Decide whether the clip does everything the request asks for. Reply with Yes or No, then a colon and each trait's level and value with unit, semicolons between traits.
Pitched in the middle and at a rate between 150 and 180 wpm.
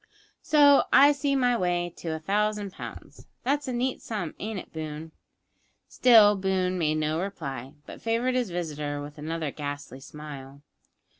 Yes: medium, 175 Hz; average, 155 wpm